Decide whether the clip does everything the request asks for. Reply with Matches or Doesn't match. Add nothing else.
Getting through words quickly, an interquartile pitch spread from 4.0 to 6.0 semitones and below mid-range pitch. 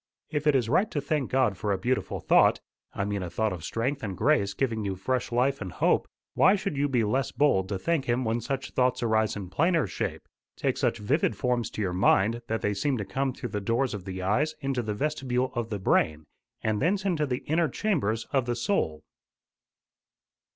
Matches